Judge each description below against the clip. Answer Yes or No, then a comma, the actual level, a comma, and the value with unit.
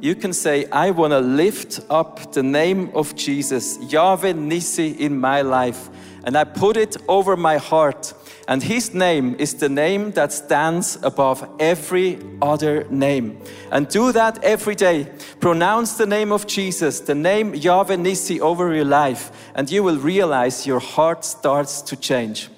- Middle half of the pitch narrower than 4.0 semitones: No, average, 5.1 semitones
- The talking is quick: No, average, 165 wpm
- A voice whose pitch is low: No, medium, 155 Hz